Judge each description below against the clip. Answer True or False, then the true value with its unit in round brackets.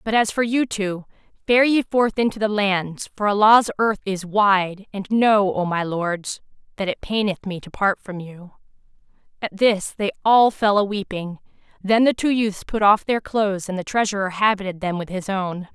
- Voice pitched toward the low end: False (200 Hz)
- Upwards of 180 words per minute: True (200 wpm)